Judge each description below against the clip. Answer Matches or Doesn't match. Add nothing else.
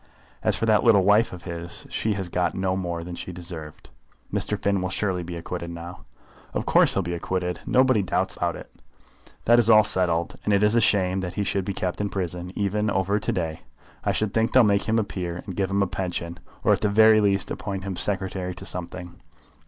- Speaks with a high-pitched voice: Doesn't match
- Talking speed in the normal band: Doesn't match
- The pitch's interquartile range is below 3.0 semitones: Matches